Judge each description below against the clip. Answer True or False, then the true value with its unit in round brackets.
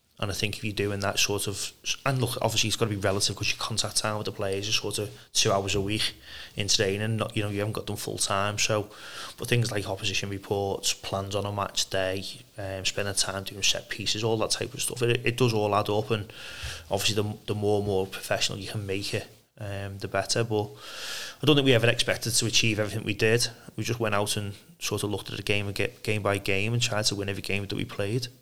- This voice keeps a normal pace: False (260 wpm)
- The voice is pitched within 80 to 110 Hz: True (105 Hz)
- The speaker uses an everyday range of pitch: False (2.1 semitones)